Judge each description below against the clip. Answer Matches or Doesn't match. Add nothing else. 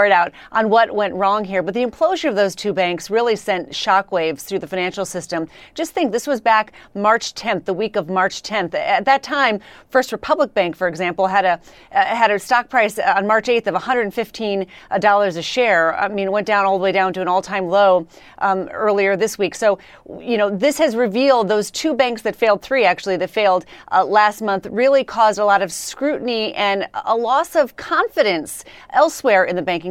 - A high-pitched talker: Matches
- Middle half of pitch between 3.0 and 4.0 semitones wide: Matches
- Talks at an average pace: Doesn't match